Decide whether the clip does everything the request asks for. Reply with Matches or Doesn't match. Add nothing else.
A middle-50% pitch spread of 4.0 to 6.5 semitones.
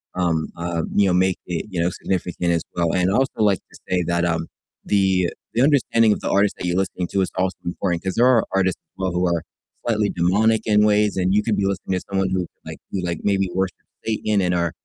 Doesn't match